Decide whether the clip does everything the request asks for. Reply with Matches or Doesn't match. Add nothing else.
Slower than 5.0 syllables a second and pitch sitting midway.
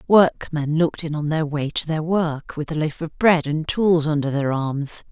Matches